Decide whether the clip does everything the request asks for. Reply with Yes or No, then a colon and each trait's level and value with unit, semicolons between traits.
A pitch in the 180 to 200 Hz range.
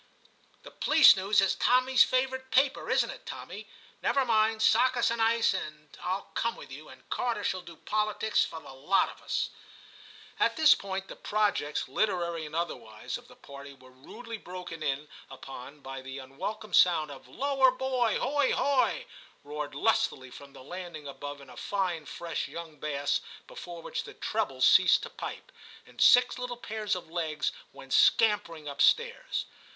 Yes: medium, 185 Hz